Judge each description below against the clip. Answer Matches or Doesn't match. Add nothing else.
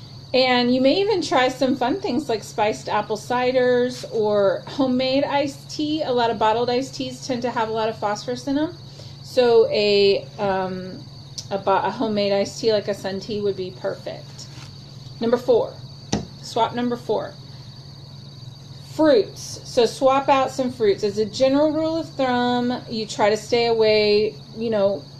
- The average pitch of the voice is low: Doesn't match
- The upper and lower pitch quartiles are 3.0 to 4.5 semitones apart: Doesn't match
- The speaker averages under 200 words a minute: Matches